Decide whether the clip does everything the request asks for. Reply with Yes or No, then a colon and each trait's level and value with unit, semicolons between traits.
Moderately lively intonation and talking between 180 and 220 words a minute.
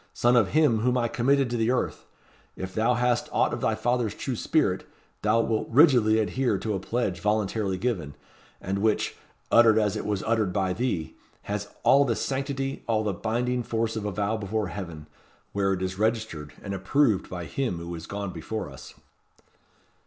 Yes: average, 3.9 semitones; average, 185 wpm